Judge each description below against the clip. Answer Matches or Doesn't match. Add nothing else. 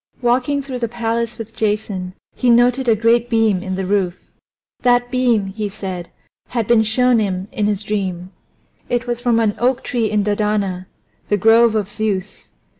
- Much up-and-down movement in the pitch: Doesn't match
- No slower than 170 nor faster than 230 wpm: Matches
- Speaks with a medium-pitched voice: Doesn't match